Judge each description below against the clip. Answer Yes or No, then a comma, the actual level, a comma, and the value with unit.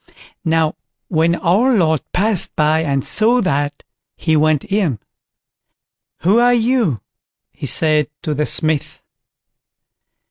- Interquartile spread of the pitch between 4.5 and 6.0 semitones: Yes, average, 5.2 semitones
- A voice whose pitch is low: No, medium, 160 Hz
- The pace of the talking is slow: Yes, slow, 120 wpm